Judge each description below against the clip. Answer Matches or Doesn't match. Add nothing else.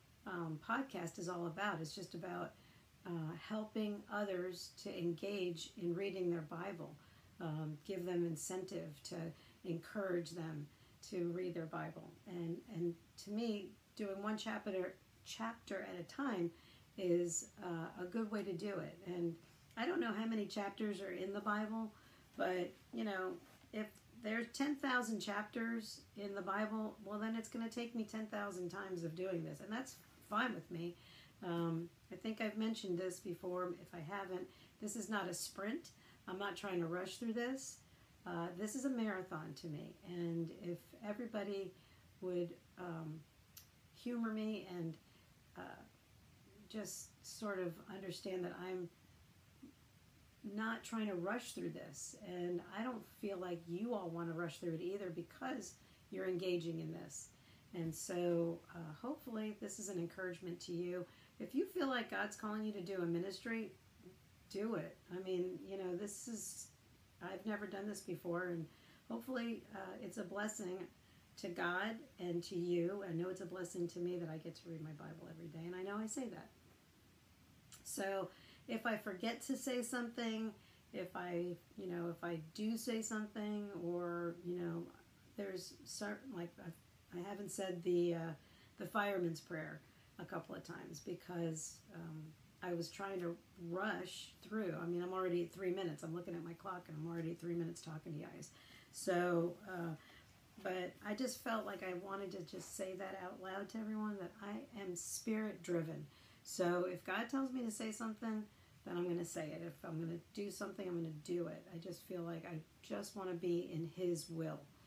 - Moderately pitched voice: Matches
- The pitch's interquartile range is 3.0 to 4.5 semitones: Matches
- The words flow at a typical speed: Matches